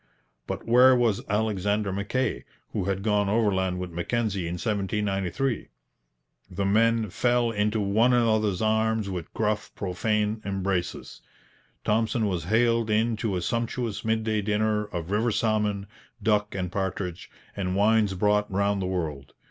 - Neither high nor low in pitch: No, low, 105 Hz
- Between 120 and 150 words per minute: Yes, average, 140 wpm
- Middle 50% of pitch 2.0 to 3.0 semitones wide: Yes, narrow, 2.4 semitones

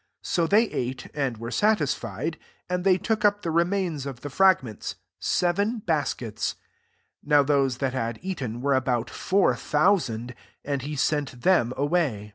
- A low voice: No, medium, 145 Hz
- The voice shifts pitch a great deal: Yes, wide, 6.1 semitones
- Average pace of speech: Yes, average, 170 wpm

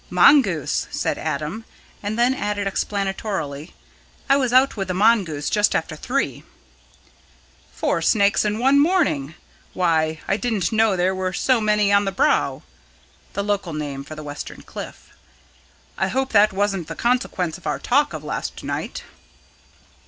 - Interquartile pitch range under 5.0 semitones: No, average, 5.3 semitones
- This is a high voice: Yes, high, 200 Hz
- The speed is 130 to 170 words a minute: Yes, average, 150 wpm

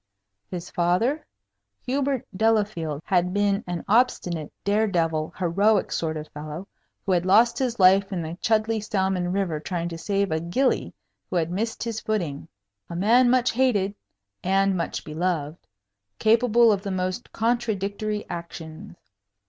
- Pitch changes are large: No, average, 4.2 semitones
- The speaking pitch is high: Yes, high, 195 Hz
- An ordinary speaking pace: Yes, average, 145 wpm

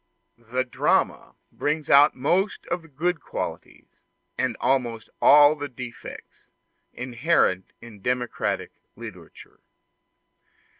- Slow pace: Yes, slow, 100 wpm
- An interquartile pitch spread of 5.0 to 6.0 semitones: No, average, 4.0 semitones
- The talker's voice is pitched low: Yes, low, 130 Hz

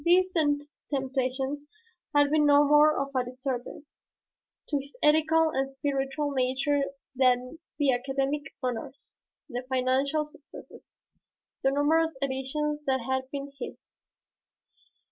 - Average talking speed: No, slow, 115 wpm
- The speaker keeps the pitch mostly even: Yes, narrow, 2.1 semitones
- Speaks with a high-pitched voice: Yes, very high, 275 Hz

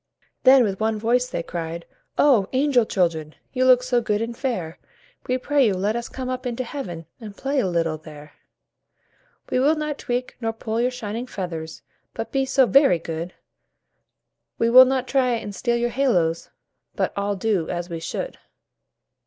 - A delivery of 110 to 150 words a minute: No, average, 180 wpm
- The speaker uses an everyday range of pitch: No, wide, 6.1 semitones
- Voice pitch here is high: Yes, high, 230 Hz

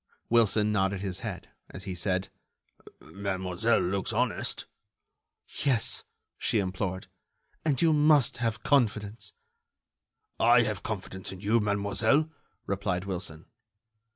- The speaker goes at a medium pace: No, slow, 110 wpm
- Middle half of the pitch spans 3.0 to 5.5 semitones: Yes, average, 3.7 semitones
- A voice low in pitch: Yes, low, 105 Hz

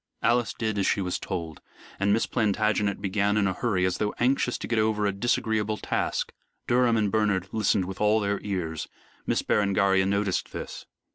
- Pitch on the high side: No, low, 105 Hz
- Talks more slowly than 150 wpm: No, average, 185 wpm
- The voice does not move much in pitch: Yes, narrow, 2.1 semitones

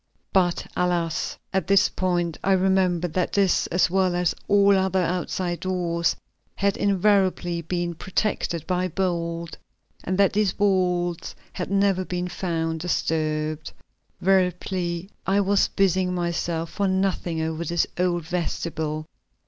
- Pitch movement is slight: Yes, narrow, 2.0 semitones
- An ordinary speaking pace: No, slow, 130 wpm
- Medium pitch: Yes, medium, 180 Hz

